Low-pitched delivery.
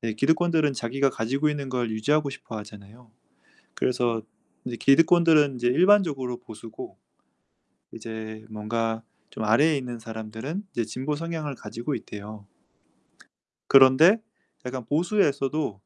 Yes: low, 125 Hz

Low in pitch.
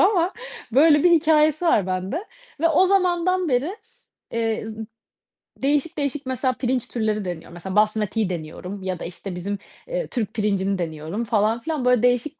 No: high, 240 Hz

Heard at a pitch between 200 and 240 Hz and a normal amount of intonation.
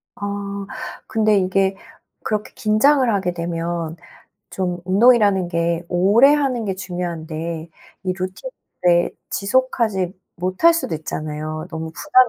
No: medium, 185 Hz; average, 3.9 semitones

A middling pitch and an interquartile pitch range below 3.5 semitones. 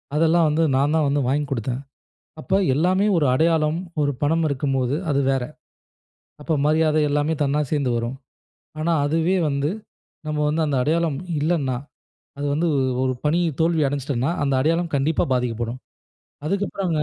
Yes: medium, 150 Hz; average, 2.9 semitones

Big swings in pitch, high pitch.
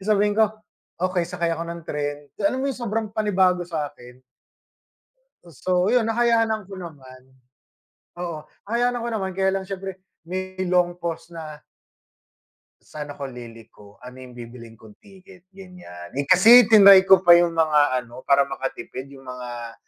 No: wide, 6.0 semitones; medium, 175 Hz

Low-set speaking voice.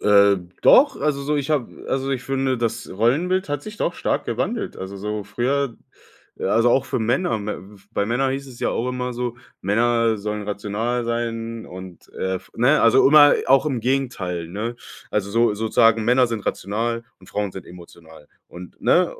Yes: low, 115 Hz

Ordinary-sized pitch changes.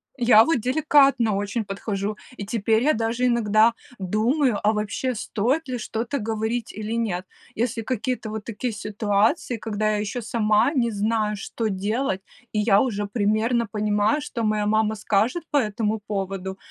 No: narrow, 2.3 semitones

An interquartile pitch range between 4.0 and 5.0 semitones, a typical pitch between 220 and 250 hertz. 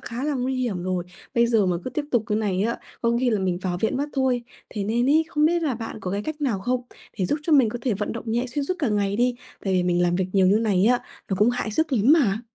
Yes: average, 4.7 semitones; high, 230 Hz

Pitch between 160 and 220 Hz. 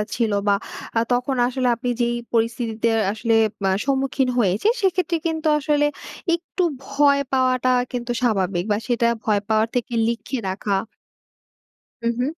No: high, 245 Hz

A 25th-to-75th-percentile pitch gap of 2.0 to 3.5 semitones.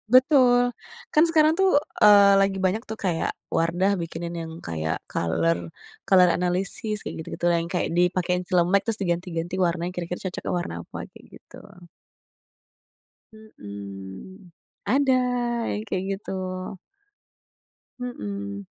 No: average, 4.1 semitones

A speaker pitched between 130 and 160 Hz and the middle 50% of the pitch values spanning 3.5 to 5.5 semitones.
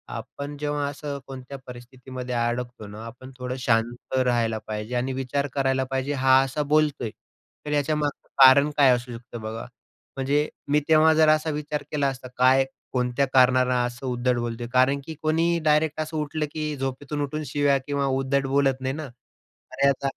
No: low, 135 Hz; average, 2.7 semitones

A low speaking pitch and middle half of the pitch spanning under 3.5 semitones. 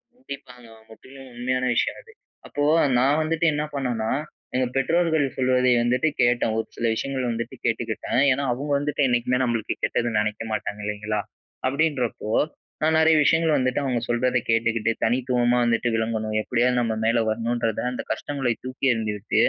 Yes: low, 125 Hz; average, 3.1 semitones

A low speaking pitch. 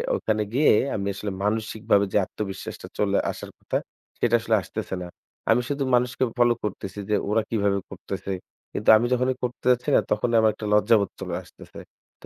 Yes: low, 110 Hz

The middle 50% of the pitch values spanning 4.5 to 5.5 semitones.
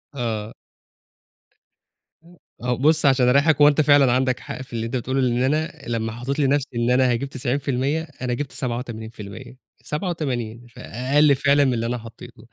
No: average, 3.0 semitones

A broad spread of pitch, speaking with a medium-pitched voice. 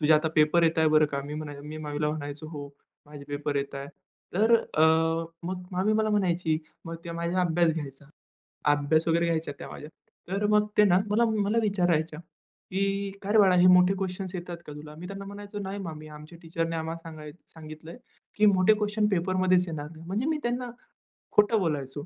No: average, 4.3 semitones; medium, 170 Hz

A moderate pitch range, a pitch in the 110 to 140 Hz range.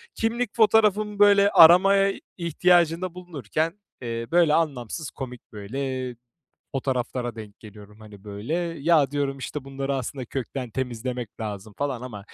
No: wide, 6.5 semitones; low, 135 Hz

